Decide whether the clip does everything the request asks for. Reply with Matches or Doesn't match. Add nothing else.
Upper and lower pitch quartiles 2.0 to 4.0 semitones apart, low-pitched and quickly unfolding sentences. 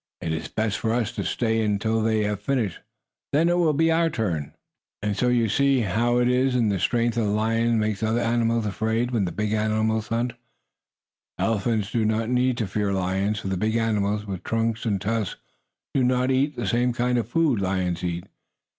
Matches